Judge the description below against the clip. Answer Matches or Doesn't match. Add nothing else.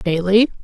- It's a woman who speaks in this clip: Matches